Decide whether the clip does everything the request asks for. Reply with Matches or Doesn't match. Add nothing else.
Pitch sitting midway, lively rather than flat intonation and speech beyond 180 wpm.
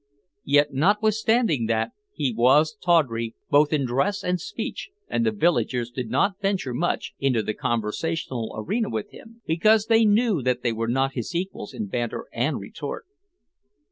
Doesn't match